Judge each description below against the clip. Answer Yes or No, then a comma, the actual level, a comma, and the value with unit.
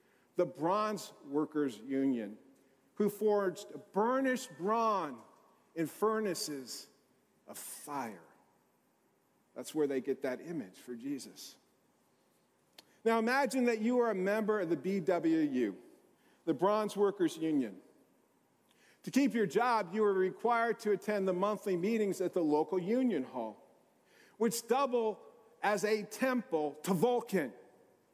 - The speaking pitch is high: Yes, high, 205 Hz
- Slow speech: Yes, slow, 125 wpm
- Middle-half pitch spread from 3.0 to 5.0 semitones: No, wide, 5.4 semitones